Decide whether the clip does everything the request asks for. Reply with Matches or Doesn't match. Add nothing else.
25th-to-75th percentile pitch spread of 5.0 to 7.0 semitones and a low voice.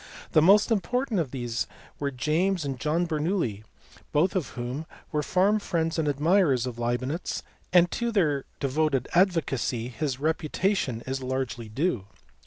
Doesn't match